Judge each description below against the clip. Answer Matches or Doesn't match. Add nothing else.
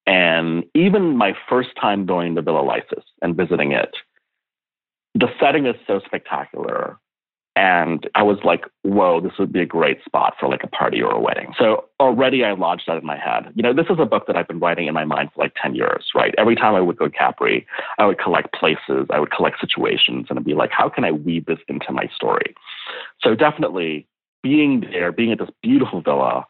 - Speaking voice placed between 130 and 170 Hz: Doesn't match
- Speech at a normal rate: Doesn't match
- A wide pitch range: Matches